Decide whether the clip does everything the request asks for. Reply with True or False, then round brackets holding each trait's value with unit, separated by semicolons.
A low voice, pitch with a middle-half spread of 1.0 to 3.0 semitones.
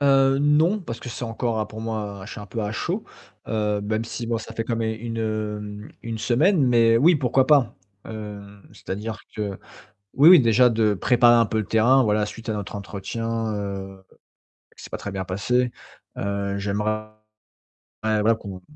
True (110 Hz; 2.5 semitones)